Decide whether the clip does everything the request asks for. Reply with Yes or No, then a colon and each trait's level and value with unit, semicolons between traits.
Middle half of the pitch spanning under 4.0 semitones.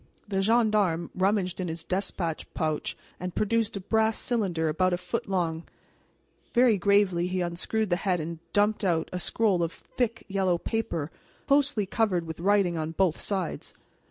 Yes: average, 3.6 semitones